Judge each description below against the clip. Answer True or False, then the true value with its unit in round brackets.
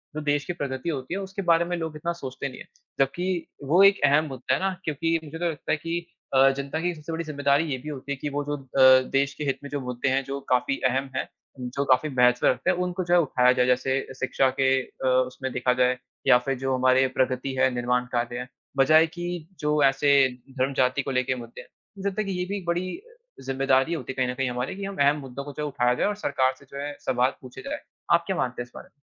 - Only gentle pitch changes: False (4.1 semitones)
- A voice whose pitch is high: False (140 Hz)